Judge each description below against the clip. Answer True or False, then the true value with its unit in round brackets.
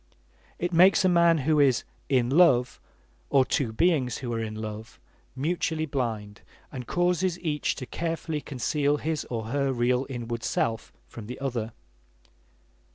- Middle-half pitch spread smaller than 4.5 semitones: False (5.2 semitones)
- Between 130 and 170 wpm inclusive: True (150 wpm)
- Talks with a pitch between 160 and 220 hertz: False (135 Hz)